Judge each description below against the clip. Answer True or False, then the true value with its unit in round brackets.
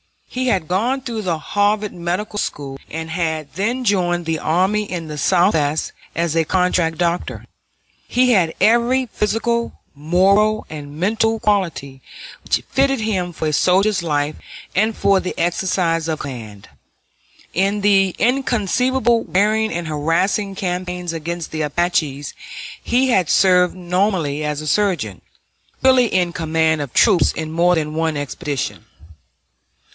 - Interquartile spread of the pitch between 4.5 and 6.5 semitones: True (4.9 semitones)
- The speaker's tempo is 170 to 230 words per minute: False (140 wpm)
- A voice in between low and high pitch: True (180 Hz)